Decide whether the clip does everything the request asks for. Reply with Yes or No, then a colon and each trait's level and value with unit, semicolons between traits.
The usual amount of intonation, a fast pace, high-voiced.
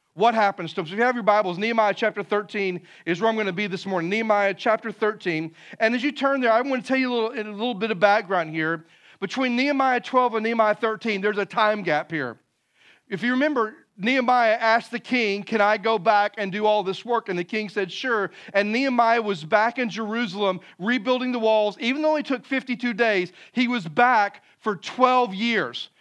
Yes: average, 3.3 semitones; fast, 220 wpm; high, 220 Hz